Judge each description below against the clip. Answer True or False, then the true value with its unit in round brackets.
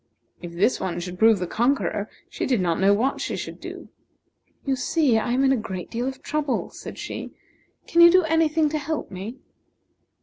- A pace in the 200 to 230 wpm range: True (205 wpm)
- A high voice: True (250 Hz)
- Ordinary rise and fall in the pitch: False (7.6 semitones)